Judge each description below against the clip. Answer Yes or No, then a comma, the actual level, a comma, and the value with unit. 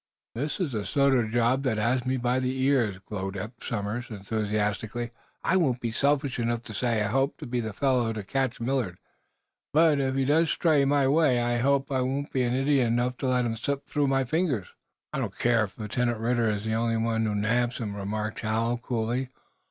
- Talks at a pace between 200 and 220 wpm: Yes, fast, 205 wpm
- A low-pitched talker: Yes, low, 120 Hz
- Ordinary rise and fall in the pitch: Yes, average, 3.3 semitones